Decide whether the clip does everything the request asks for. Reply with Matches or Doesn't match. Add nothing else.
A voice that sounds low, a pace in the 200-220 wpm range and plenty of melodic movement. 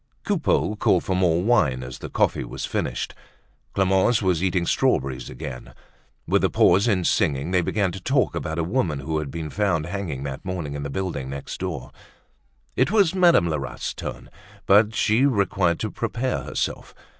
Doesn't match